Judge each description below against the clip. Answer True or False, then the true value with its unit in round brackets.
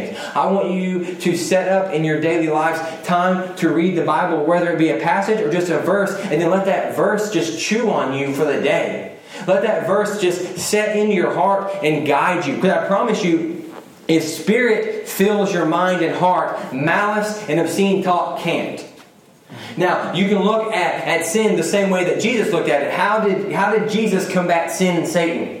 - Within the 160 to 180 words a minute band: False (205 wpm)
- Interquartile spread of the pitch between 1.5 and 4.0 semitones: True (3.4 semitones)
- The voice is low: False (180 Hz)